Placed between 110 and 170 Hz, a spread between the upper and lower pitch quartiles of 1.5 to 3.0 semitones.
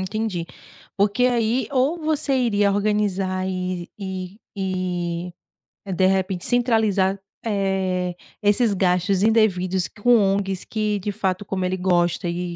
No: high, 195 Hz; average, 2.7 semitones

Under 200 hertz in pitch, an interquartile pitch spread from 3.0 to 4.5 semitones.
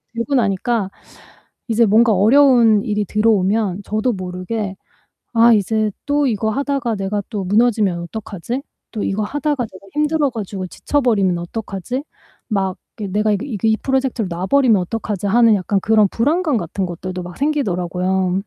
No: high, 215 Hz; average, 4.0 semitones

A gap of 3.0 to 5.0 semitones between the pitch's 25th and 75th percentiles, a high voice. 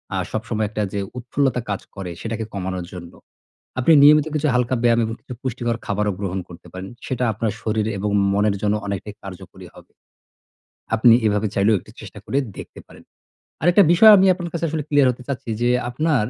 No: average, 4.6 semitones; low, 115 Hz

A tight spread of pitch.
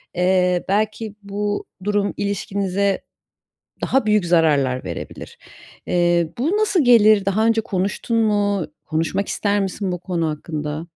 No: average, 3.4 semitones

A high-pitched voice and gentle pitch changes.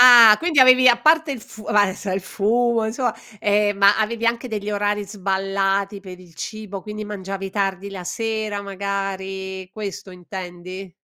Yes: high, 205 Hz; narrow, 2.3 semitones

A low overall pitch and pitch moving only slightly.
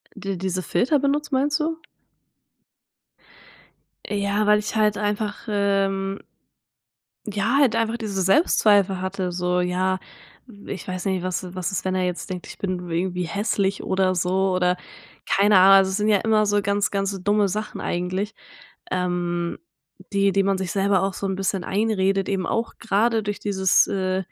No: high, 195 Hz; narrow, 2.1 semitones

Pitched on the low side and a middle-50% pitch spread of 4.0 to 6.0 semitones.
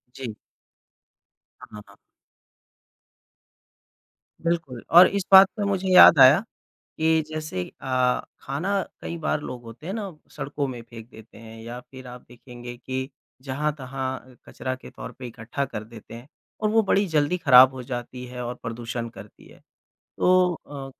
Yes: low, 130 Hz; average, 4.7 semitones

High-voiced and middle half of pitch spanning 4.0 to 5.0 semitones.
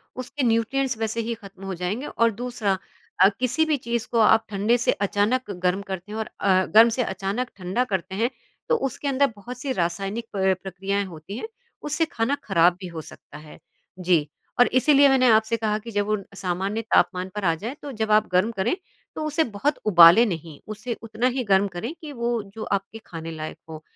Yes: high, 215 Hz; average, 4.4 semitones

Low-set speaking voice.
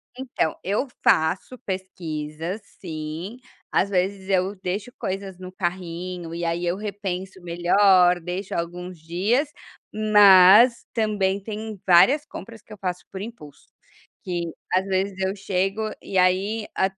No: high, 190 Hz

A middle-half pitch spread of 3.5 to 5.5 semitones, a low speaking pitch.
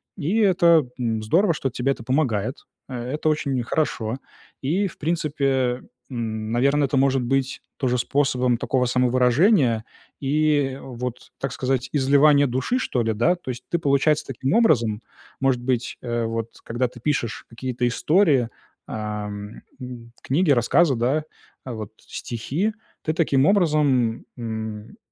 Yes: average, 3.9 semitones; low, 130 Hz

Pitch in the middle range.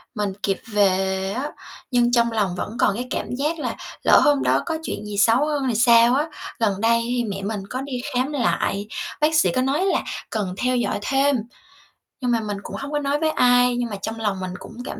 No: high, 240 Hz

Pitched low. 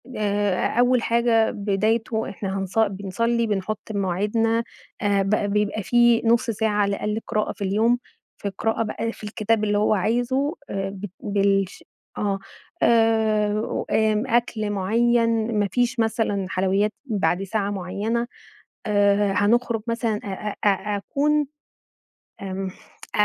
No: high, 215 Hz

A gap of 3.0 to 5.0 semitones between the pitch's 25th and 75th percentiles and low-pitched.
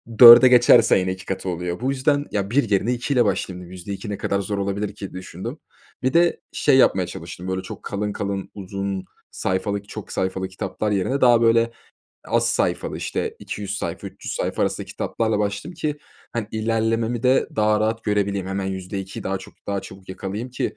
Yes: average, 3.4 semitones; low, 100 Hz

